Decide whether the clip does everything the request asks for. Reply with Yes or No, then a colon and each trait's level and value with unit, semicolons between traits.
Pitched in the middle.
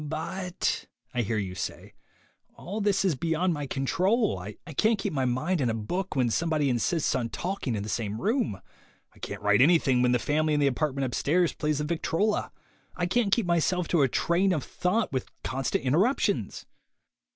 Yes: medium, 155 Hz